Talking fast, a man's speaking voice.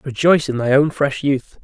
Yes: fast, 220 wpm; male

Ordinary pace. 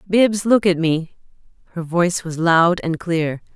Yes: average, 170 wpm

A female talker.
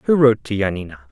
No: male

